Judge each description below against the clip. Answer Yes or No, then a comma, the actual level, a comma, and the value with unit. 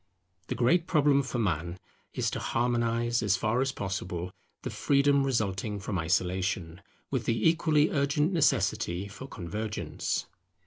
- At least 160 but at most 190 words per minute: No, slow, 135 wpm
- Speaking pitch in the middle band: No, low, 115 Hz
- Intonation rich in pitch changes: Yes, wide, 6.6 semitones